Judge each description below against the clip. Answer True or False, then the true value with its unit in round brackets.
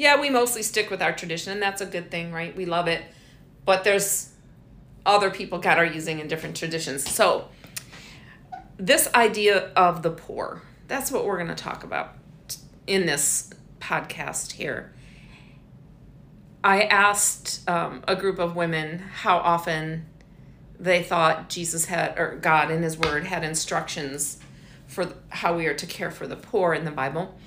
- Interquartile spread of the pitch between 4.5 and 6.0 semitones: False (3.1 semitones)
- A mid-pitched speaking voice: True (175 Hz)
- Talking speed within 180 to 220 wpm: False (165 wpm)